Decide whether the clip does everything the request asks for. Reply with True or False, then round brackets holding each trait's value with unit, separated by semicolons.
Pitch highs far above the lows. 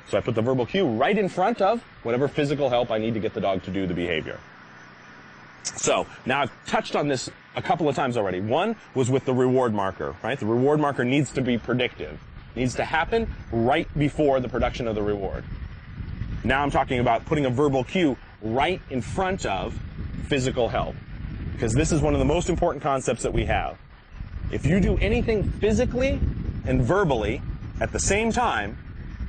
False (5.0 semitones)